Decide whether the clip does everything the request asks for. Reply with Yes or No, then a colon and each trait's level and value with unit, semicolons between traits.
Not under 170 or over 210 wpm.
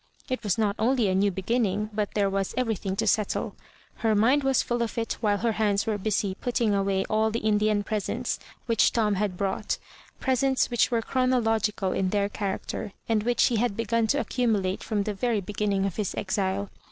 Yes: average, 200 wpm